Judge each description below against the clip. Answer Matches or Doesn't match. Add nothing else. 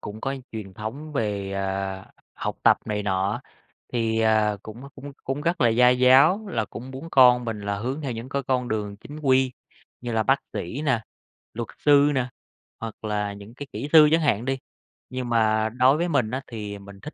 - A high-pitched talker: Doesn't match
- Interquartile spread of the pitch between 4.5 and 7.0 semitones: Doesn't match